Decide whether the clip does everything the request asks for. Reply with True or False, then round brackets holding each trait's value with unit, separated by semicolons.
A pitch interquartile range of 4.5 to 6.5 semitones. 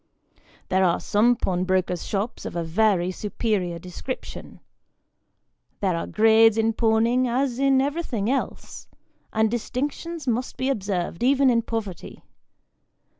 True (5.0 semitones)